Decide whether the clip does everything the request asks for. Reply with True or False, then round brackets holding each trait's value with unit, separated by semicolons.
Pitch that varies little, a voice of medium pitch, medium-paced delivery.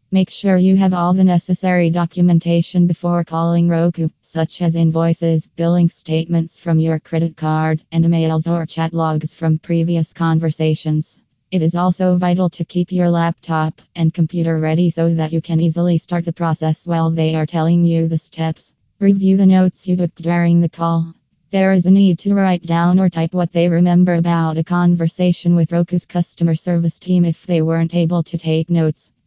True (1.4 semitones; 170 Hz; 180 wpm)